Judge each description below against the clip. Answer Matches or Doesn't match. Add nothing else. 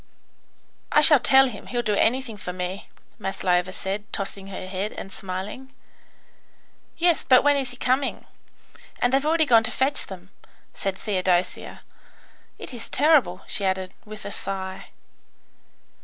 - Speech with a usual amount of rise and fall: Doesn't match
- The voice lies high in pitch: Matches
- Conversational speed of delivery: Matches